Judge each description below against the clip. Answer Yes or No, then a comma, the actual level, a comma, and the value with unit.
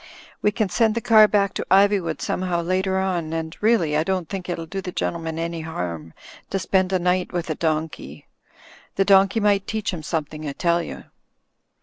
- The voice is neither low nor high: Yes, medium, 180 Hz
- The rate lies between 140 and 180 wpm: No, average, 195 wpm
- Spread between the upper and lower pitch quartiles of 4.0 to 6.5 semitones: No, average, 3.2 semitones